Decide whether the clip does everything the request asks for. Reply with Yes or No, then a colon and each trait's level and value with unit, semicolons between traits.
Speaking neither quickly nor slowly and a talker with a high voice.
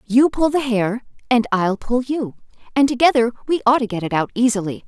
No: fast, 210 wpm; high, 240 Hz